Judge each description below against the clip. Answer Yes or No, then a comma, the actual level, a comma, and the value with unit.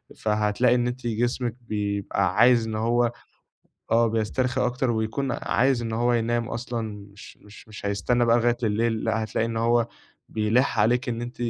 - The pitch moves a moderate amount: No, narrow, 1.8 semitones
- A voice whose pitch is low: Yes, low, 115 Hz